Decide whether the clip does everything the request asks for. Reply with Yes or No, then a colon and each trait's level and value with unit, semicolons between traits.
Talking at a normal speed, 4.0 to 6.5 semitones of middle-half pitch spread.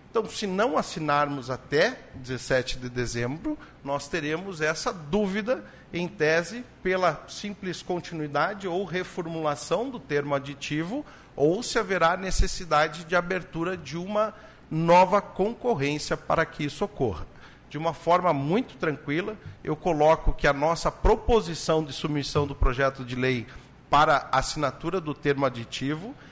Yes: average, 130 wpm; average, 4.4 semitones